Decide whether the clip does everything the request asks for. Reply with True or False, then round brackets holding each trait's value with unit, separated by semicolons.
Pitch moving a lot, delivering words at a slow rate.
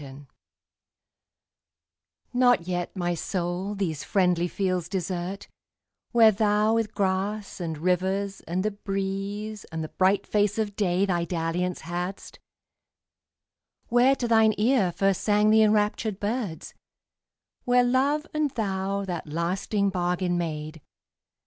False (3.2 semitones; 125 wpm)